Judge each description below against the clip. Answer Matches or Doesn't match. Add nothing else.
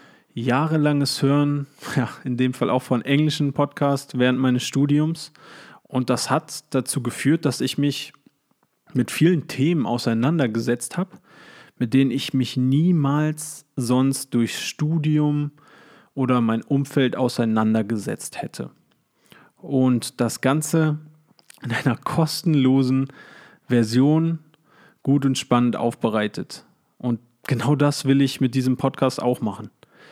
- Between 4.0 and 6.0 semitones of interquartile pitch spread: Doesn't match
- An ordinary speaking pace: Doesn't match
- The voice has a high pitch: Doesn't match